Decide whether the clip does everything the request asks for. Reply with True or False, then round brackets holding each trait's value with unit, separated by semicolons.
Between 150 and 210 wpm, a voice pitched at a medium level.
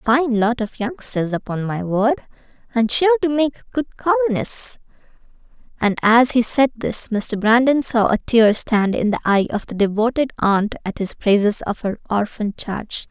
False (180 wpm; 230 Hz)